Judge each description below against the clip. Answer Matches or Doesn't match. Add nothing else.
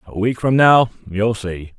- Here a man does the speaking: Matches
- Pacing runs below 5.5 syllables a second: Matches